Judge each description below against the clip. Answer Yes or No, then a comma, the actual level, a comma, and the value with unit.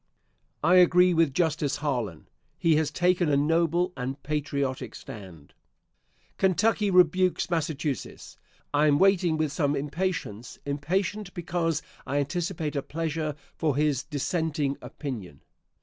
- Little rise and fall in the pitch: No, average, 3.8 semitones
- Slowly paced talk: Yes, slow, 120 wpm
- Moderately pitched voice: Yes, medium, 155 Hz